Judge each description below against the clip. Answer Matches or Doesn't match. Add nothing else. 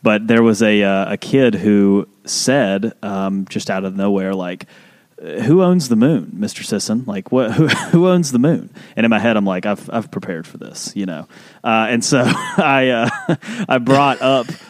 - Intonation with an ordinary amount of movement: Doesn't match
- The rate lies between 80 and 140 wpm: Doesn't match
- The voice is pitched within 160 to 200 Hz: Doesn't match